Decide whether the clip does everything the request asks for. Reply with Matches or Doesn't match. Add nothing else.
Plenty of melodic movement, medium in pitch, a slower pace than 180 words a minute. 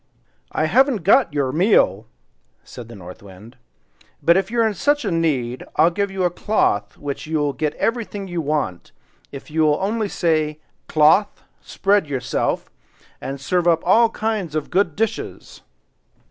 Matches